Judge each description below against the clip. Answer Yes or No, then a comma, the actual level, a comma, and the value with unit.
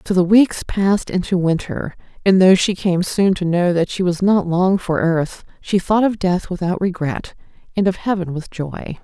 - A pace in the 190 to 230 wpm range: Yes, fast, 205 wpm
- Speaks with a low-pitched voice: No, medium, 185 Hz